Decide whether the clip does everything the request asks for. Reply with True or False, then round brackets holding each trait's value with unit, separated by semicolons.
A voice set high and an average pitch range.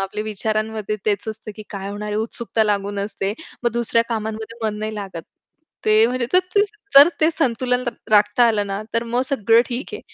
False (220 Hz; 2.3 semitones)